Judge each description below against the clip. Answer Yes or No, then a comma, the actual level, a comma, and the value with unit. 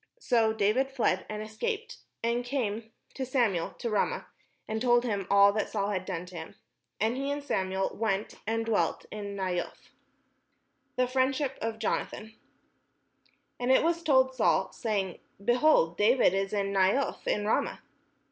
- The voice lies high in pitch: Yes, high, 220 Hz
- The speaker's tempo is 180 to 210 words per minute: No, average, 155 wpm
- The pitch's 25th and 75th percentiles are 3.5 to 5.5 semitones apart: Yes, average, 4.4 semitones